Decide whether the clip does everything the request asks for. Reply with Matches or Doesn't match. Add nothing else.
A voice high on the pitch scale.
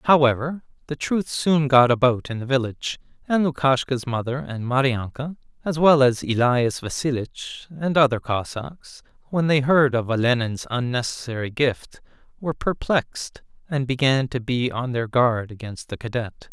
Doesn't match